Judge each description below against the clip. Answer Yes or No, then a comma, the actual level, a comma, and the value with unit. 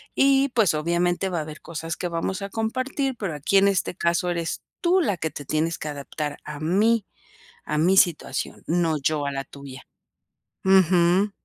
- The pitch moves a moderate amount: Yes, average, 4.3 semitones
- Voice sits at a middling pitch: Yes, medium, 170 Hz